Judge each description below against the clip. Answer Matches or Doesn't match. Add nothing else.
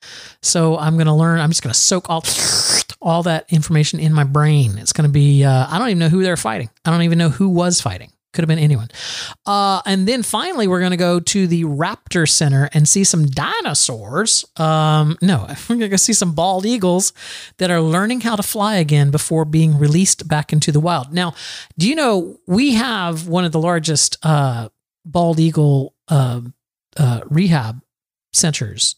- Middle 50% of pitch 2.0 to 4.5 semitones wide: Matches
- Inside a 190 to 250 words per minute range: Matches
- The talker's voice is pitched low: Doesn't match